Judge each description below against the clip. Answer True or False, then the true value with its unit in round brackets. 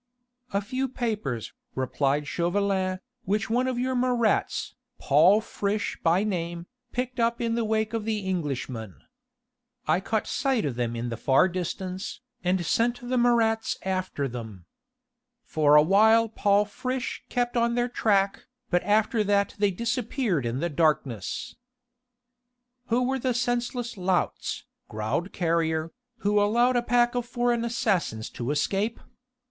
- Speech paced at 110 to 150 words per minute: True (140 wpm)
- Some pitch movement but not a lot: False (6.1 semitones)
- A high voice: True (205 Hz)